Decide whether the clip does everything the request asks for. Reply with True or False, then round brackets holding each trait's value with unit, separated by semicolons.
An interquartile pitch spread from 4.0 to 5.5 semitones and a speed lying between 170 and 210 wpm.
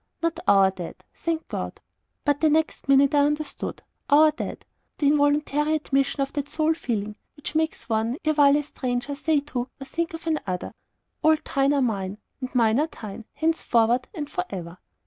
True (4.5 semitones; 175 wpm)